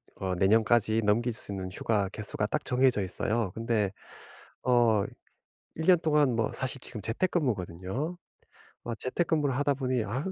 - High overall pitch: No, low, 115 Hz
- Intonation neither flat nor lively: Yes, average, 4.3 semitones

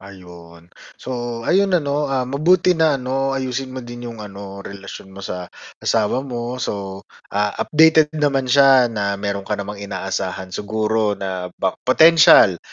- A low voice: Yes, low, 115 Hz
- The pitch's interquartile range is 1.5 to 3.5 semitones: No, wide, 5.5 semitones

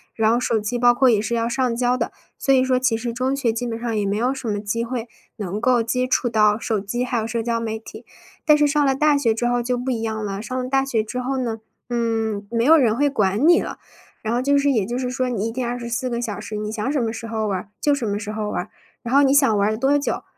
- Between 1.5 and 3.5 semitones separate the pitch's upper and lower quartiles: Yes, average, 2.7 semitones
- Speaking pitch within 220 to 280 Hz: Yes, high, 235 Hz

